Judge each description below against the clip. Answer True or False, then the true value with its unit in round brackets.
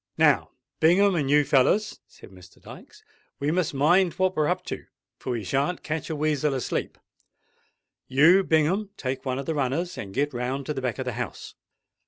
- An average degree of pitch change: True (4.3 semitones)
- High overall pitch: False (150 Hz)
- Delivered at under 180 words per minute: False (190 wpm)